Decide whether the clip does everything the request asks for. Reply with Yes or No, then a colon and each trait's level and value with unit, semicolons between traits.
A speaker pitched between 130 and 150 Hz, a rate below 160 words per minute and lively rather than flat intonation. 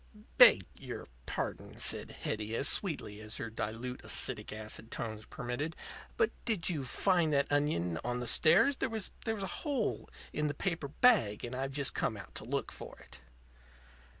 No: medium, 140 Hz; average, 170 wpm; wide, 7.8 semitones